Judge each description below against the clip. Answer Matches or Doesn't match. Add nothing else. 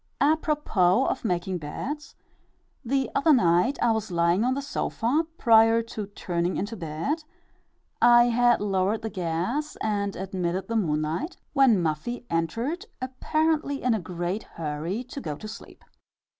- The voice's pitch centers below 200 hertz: Doesn't match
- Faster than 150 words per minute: Doesn't match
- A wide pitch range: Matches